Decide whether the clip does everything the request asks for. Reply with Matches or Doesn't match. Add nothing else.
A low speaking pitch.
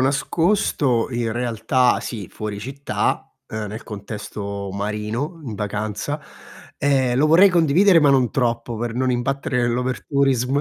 Matches